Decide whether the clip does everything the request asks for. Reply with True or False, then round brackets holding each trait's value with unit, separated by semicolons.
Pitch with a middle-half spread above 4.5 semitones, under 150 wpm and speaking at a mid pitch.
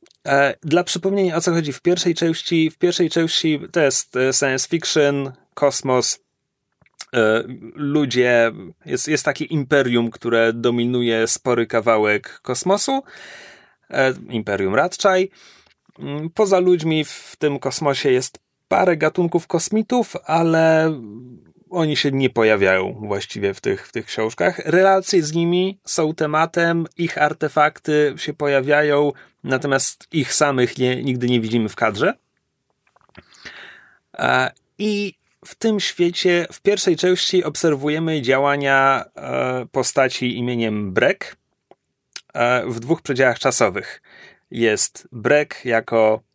True (5.3 semitones; 110 wpm; 150 Hz)